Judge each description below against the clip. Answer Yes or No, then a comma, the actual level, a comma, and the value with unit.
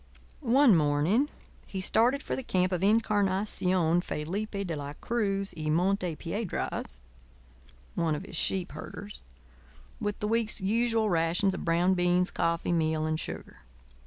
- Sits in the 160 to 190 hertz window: Yes, medium, 185 Hz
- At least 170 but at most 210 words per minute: No, average, 140 wpm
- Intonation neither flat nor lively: Yes, average, 3.9 semitones